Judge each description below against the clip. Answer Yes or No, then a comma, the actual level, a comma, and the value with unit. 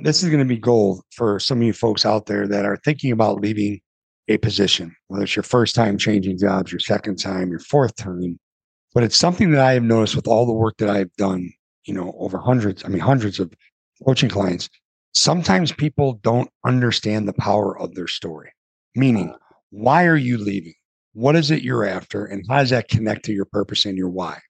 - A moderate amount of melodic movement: Yes, average, 4.2 semitones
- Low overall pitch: Yes, low, 105 Hz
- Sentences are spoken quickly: Yes, fast, 215 wpm